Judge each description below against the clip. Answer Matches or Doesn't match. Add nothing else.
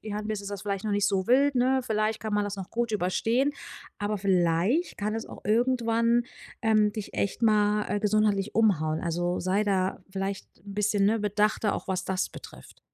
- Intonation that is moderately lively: Doesn't match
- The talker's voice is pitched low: Doesn't match